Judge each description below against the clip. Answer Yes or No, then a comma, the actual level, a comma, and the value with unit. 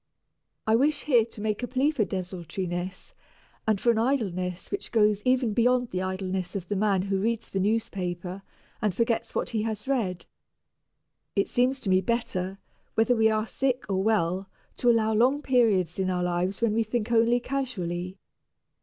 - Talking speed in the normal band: Yes, average, 175 wpm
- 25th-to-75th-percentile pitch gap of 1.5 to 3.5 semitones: No, average, 4.1 semitones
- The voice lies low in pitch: No, high, 215 Hz